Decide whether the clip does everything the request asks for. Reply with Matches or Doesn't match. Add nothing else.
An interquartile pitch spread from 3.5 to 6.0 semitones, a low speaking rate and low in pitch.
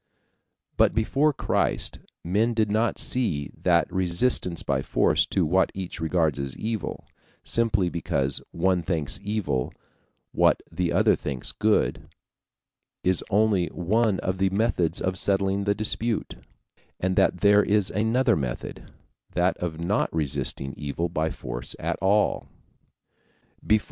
Matches